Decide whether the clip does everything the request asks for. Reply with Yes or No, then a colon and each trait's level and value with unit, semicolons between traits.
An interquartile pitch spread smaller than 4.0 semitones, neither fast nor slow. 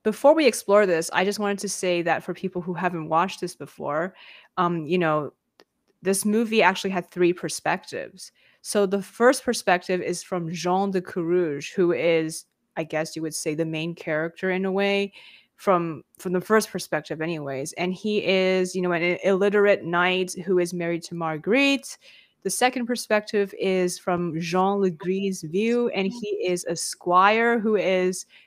Yes: average, 2.8 semitones; average, 175 wpm